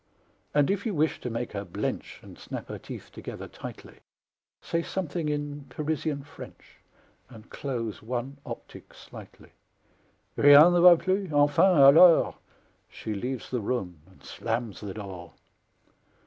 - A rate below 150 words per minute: Yes, average, 140 wpm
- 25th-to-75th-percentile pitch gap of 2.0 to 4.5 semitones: No, wide, 5.6 semitones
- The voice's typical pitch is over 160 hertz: No, medium, 140 Hz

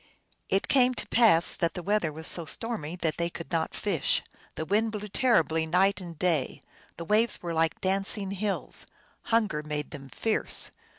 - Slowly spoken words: No, average, 175 wpm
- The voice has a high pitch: No, medium, 180 Hz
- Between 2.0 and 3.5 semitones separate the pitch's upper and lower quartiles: No, average, 4.7 semitones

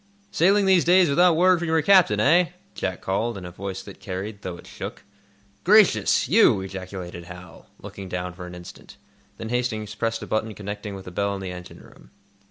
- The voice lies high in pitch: No, low, 105 Hz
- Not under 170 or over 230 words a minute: Yes, average, 190 wpm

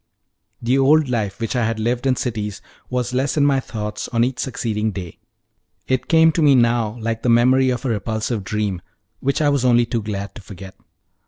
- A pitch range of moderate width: Yes, average, 3.4 semitones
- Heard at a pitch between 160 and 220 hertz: No, low, 120 Hz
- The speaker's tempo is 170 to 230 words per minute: Yes, average, 200 wpm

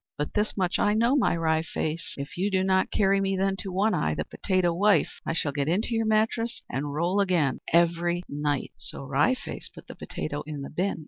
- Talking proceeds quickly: Yes, fast, 220 wpm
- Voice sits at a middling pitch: Yes, medium, 175 Hz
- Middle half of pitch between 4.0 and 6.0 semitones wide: Yes, average, 4.7 semitones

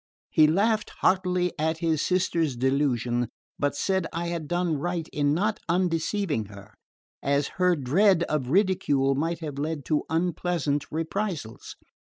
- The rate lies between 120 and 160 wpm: Yes, average, 140 wpm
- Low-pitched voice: No, medium, 160 Hz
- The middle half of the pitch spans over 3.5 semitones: Yes, average, 4.0 semitones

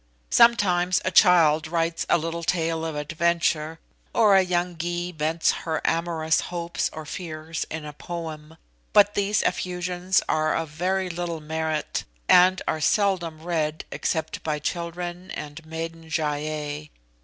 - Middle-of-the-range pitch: Yes, medium, 165 Hz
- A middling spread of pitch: No, narrow, 2.2 semitones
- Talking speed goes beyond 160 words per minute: No, average, 145 wpm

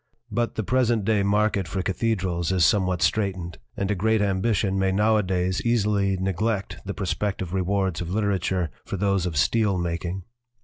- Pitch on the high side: No, very low, 95 Hz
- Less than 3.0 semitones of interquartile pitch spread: Yes, narrow, 2.4 semitones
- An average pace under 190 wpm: Yes, average, 160 wpm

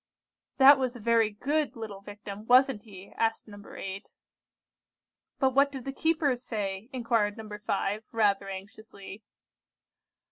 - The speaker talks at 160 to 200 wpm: No, average, 140 wpm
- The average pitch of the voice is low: No, high, 220 Hz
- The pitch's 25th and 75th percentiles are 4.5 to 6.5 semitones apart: No, average, 4.1 semitones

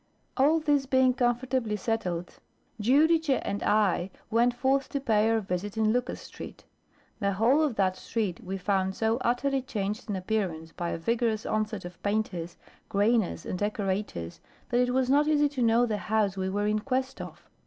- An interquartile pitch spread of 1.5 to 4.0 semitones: No, average, 4.5 semitones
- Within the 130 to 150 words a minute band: No, average, 175 wpm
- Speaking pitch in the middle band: No, high, 220 Hz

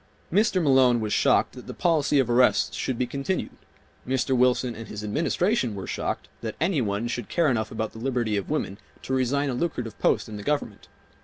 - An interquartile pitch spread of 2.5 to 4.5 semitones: Yes, average, 4.2 semitones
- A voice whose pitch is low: Yes, low, 125 Hz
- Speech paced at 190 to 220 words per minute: Yes, fast, 205 wpm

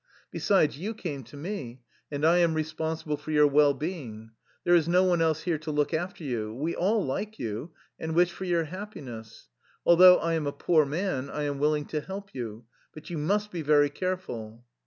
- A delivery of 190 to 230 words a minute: Yes, fast, 205 wpm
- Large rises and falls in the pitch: No, average, 3.7 semitones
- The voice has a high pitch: No, medium, 155 Hz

